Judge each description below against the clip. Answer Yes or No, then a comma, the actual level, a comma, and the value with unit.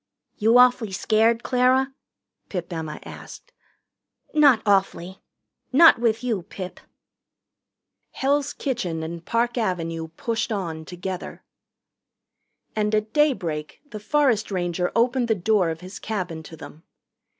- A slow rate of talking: Yes, slow, 120 wpm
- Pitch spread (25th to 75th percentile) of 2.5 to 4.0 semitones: No, wide, 5.6 semitones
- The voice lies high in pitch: Yes, high, 210 Hz